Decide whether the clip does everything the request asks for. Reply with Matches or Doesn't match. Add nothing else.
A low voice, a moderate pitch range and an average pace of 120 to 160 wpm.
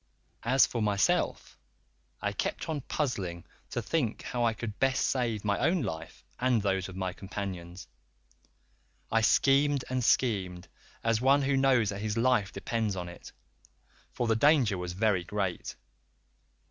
Matches